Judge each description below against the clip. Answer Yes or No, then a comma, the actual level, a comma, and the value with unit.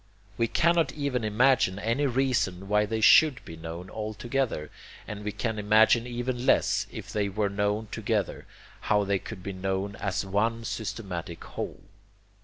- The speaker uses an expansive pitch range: No, average, 3.4 semitones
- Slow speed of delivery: No, average, 160 wpm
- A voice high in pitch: No, low, 105 Hz